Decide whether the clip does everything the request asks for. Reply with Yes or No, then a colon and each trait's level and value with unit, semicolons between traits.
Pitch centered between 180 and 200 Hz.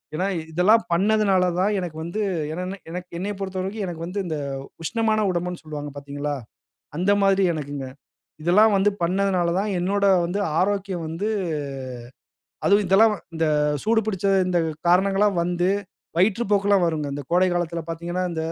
Yes: medium, 185 Hz